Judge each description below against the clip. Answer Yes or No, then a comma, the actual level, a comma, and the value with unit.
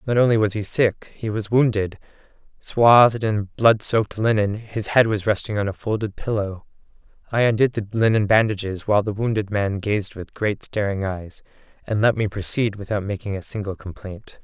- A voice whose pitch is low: Yes, low, 105 Hz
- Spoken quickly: No, average, 185 wpm